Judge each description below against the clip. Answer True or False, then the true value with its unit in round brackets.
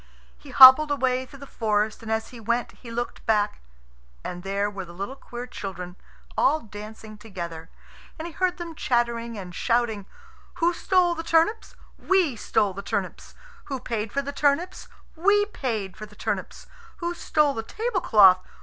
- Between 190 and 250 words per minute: False (170 wpm)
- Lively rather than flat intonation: True (6.6 semitones)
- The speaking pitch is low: False (235 Hz)